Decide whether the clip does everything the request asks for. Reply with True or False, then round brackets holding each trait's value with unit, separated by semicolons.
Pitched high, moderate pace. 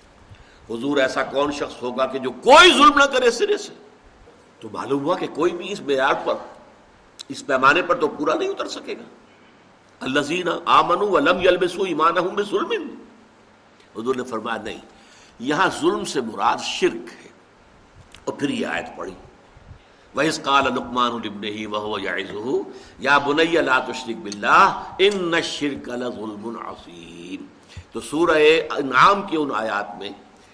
False (150 Hz; 135 wpm)